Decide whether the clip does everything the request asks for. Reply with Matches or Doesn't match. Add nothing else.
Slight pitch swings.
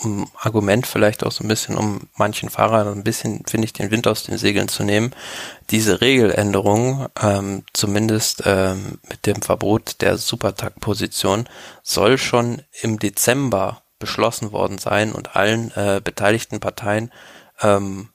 Matches